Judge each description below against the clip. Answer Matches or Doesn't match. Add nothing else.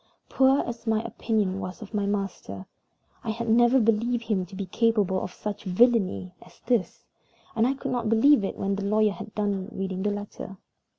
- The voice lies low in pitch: Doesn't match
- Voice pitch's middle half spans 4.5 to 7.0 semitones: Doesn't match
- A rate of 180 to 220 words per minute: Matches